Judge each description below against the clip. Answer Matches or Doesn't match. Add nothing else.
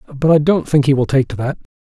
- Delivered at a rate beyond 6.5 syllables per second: Matches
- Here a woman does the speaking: Doesn't match